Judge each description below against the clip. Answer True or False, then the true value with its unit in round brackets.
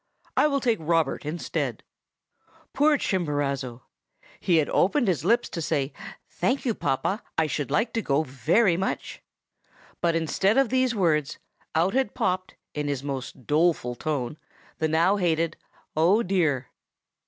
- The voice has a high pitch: False (165 Hz)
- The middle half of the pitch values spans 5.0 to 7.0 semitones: True (5.5 semitones)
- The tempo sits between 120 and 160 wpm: True (145 wpm)